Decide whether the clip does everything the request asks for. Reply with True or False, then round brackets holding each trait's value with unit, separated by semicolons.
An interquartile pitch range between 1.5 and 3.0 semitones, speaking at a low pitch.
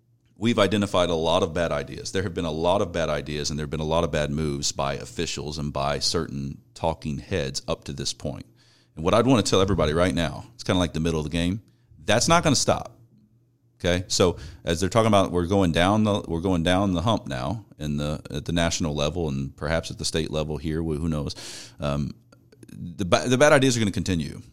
False (5.6 semitones; 85 Hz)